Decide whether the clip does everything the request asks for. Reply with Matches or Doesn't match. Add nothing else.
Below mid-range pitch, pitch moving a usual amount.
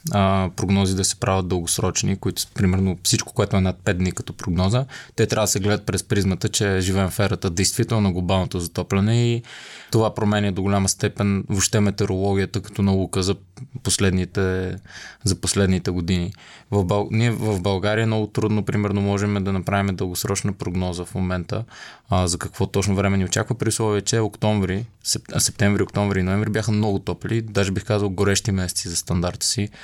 Doesn't match